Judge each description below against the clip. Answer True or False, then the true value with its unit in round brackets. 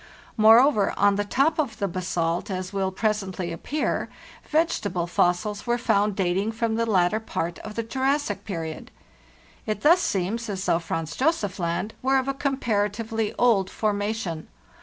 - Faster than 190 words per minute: False (155 wpm)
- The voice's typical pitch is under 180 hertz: False (210 Hz)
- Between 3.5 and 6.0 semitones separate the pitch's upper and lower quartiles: True (3.8 semitones)